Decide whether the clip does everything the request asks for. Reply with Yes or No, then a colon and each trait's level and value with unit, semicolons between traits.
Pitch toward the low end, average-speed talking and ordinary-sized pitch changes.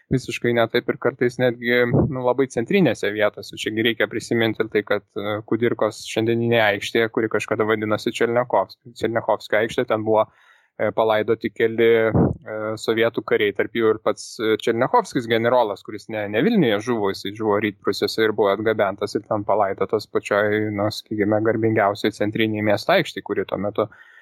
No: low, 115 Hz; average, 150 wpm; narrow, 2.1 semitones